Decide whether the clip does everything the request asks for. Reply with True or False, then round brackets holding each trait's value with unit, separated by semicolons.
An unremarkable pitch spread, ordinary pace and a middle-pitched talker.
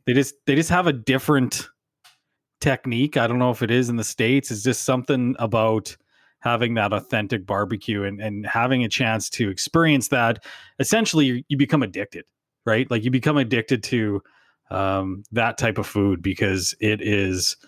False (3.9 semitones; 175 wpm; 120 Hz)